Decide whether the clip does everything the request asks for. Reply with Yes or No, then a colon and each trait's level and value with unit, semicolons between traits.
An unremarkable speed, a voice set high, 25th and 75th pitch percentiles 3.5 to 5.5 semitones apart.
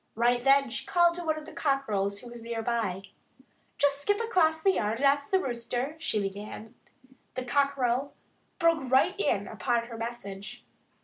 Yes: average, 180 wpm; high, 245 Hz; average, 4.2 semitones